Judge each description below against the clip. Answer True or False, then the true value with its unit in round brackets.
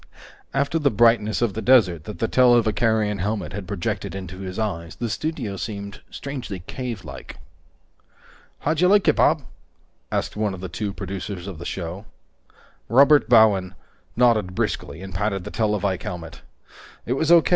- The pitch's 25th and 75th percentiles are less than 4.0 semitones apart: False (4.3 semitones)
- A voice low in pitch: True (105 Hz)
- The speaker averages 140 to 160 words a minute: True (155 wpm)